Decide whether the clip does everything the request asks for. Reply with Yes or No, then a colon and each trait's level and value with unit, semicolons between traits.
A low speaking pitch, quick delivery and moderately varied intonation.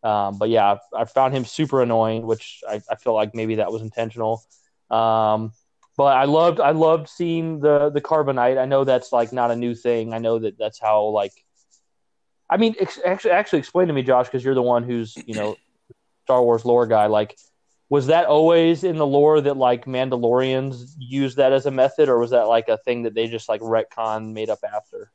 Yes: low, 120 Hz; fast, 215 wpm; average, 4.0 semitones